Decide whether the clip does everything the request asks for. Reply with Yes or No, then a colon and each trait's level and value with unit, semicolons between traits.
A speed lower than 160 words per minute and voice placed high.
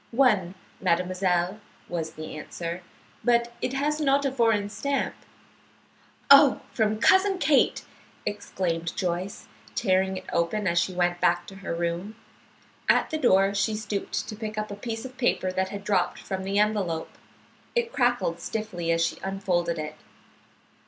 Yes: average, 150 wpm; high, 195 Hz